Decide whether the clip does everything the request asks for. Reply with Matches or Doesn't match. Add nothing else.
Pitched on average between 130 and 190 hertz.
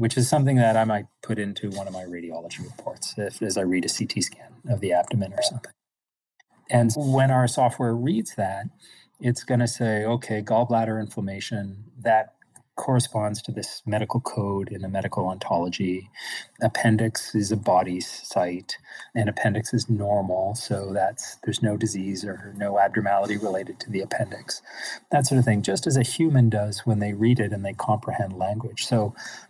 Doesn't match